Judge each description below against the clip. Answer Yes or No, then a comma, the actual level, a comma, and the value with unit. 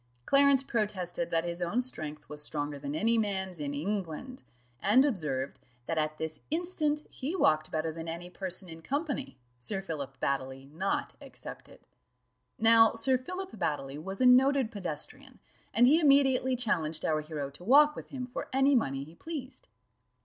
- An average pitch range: No, wide, 9.0 semitones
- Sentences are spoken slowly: No, average, 160 wpm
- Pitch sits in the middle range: No, high, 195 Hz